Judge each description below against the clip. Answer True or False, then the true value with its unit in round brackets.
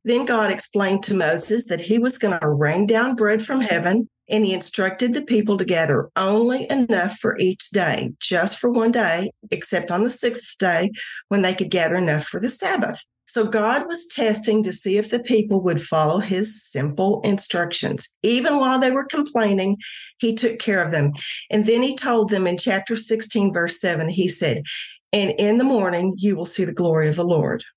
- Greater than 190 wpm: True (200 wpm)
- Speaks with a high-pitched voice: True (205 Hz)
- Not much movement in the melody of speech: False (4.3 semitones)